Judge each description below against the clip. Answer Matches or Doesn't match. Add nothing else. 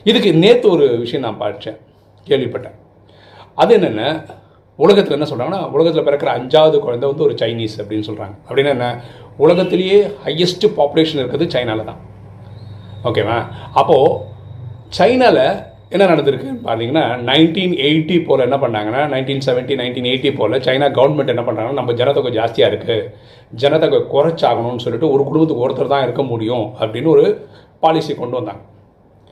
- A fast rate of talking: Matches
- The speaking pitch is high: Doesn't match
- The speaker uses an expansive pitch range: Matches